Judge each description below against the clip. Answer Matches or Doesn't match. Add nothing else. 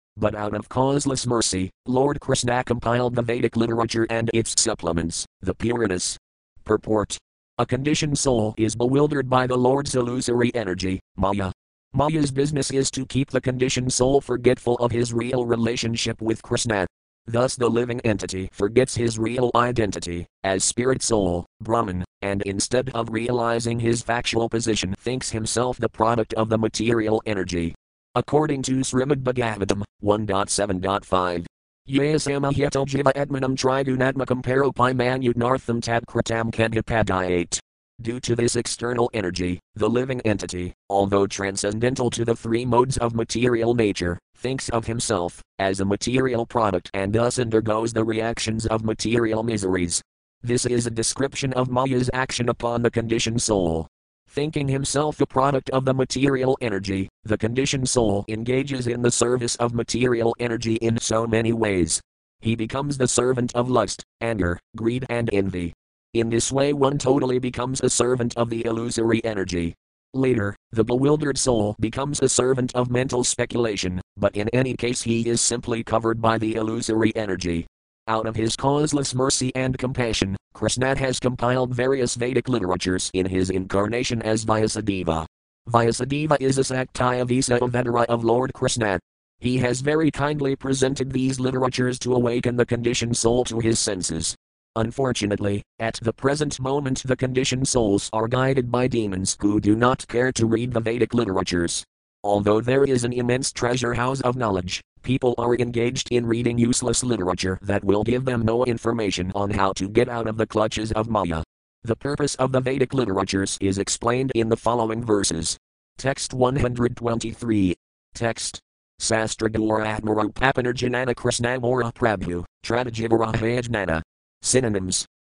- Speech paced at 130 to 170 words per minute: Matches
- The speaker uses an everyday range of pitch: Matches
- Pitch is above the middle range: Doesn't match